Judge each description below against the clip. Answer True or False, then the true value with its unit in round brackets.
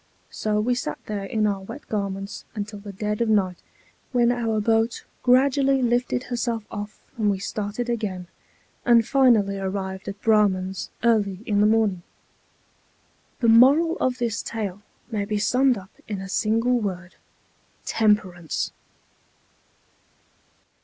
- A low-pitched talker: False (215 Hz)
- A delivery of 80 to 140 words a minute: True (135 wpm)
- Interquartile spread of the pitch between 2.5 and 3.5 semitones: True (3.1 semitones)